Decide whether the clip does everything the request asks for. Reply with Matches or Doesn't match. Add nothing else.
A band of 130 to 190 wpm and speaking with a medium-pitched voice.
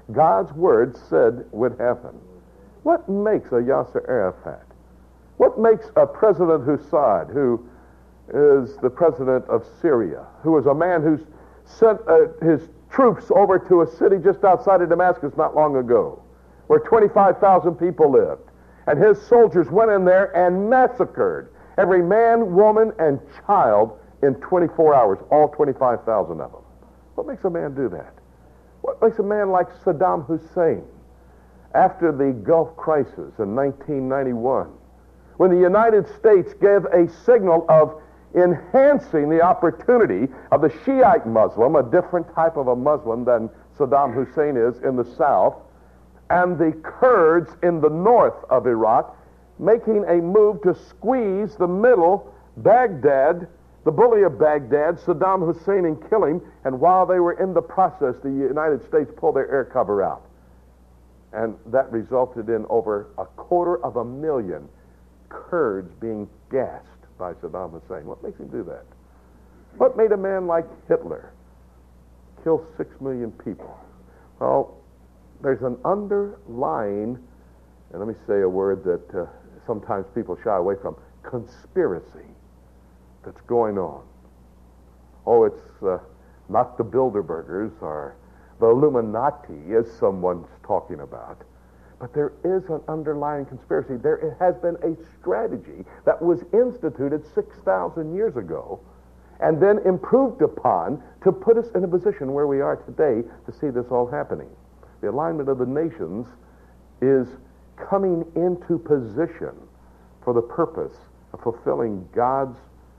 Matches